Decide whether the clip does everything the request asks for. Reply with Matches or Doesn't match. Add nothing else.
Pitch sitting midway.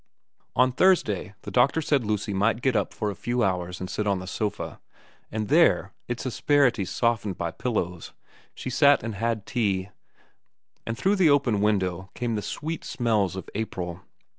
Doesn't match